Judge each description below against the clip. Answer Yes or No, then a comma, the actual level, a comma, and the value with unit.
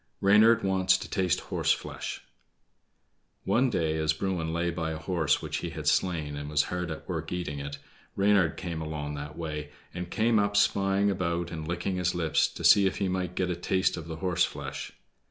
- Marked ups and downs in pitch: No, average, 3.2 semitones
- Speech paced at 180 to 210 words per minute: Yes, average, 200 wpm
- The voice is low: Yes, very low, 85 Hz